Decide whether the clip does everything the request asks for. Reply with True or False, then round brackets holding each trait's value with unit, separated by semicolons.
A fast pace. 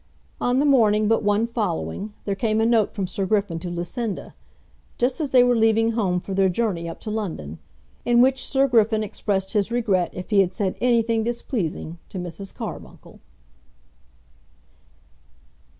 False (165 wpm)